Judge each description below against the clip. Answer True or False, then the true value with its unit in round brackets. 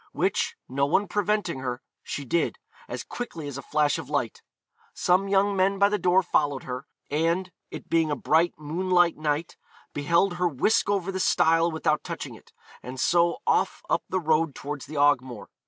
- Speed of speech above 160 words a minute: True (180 wpm)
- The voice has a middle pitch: True (165 Hz)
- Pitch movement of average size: True (4.2 semitones)